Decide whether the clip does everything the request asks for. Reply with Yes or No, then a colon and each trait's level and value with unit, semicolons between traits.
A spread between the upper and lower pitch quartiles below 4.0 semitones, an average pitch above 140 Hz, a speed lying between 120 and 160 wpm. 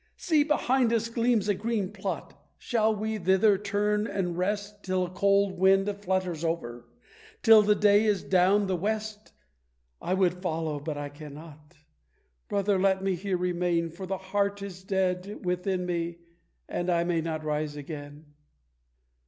Yes: average, 3.3 semitones; high, 190 Hz; average, 155 wpm